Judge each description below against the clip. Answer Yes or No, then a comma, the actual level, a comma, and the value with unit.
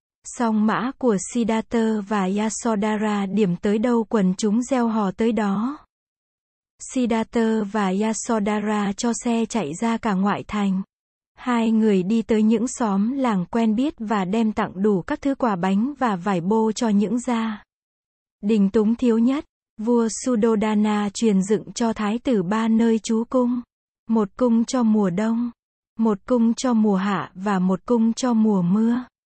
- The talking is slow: Yes, slow, 160 wpm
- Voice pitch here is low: No, high, 225 Hz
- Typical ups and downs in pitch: No, narrow, 2.0 semitones